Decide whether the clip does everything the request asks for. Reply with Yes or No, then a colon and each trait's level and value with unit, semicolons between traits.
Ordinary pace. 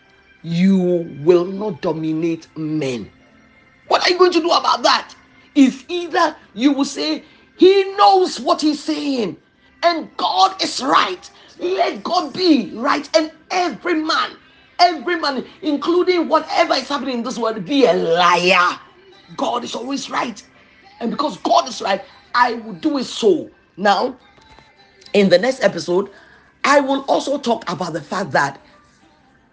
Yes: average, 150 wpm